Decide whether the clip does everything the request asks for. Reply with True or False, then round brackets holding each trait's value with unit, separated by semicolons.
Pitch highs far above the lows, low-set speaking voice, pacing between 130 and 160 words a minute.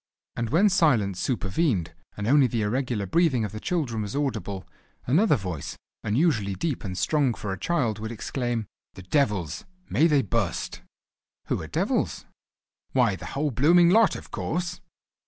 True (6.8 semitones; 120 Hz; 155 wpm)